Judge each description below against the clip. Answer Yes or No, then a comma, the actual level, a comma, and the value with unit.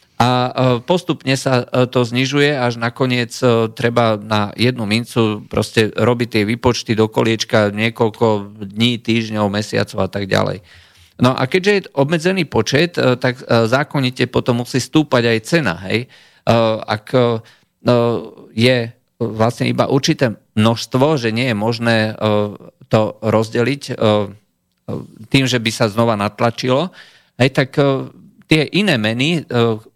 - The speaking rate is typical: Yes, average, 120 wpm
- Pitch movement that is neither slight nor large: Yes, average, 3.0 semitones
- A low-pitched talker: Yes, low, 120 Hz